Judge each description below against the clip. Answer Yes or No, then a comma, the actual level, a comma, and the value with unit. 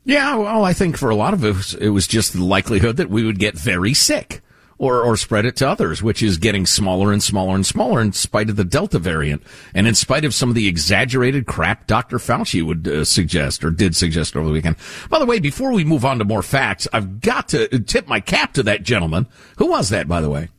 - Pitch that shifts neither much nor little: No, wide, 6.0 semitones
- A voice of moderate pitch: No, low, 110 Hz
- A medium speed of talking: No, fast, 250 wpm